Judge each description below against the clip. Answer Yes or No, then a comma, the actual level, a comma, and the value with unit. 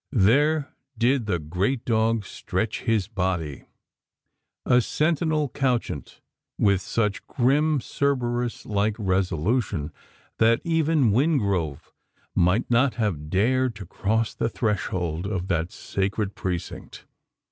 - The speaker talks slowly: Yes, slow, 110 wpm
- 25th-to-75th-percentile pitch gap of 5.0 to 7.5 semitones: Yes, average, 5.3 semitones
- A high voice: No, low, 110 Hz